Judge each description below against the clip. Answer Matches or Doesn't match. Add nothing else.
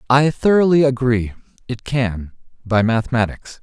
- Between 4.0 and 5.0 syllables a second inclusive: Matches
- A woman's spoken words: Doesn't match